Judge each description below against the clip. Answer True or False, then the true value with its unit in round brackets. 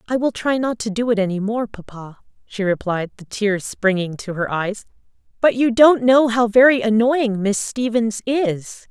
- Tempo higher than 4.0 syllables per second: True (4.5 syllables/s)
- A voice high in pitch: True (220 Hz)